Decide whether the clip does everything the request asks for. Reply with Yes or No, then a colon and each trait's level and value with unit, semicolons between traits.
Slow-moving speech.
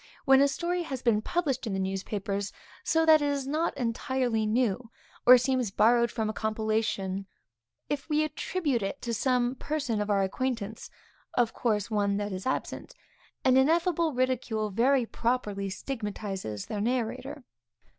No: average, 160 wpm